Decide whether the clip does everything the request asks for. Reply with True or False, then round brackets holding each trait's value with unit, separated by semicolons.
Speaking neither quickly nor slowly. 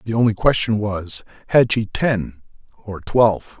True (150 wpm)